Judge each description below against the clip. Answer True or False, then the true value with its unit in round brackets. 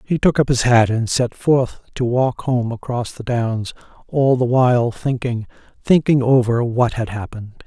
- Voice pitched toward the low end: True (125 Hz)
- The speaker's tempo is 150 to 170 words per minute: False (180 wpm)